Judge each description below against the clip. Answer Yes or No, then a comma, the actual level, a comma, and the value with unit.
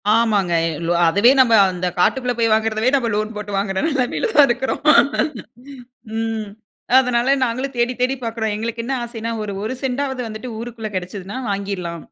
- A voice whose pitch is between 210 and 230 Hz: Yes, high, 225 Hz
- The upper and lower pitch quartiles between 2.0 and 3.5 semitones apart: Yes, average, 3.2 semitones